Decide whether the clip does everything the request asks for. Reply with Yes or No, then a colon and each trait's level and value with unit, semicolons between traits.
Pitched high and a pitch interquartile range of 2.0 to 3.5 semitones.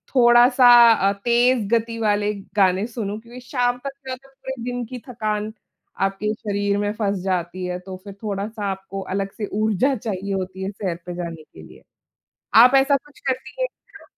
No: high, 210 Hz; average, 3.9 semitones